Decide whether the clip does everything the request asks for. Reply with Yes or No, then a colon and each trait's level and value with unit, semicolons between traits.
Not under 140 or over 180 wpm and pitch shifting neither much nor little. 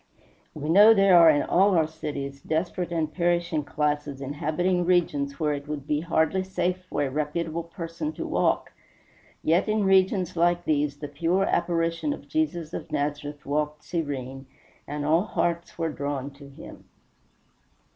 Yes: average, 155 wpm; average, 3.1 semitones